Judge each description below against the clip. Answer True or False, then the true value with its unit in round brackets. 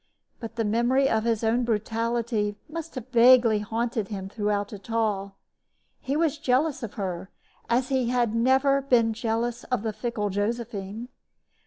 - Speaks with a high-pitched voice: True (230 Hz)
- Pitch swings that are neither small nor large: True (3.0 semitones)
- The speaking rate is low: False (155 wpm)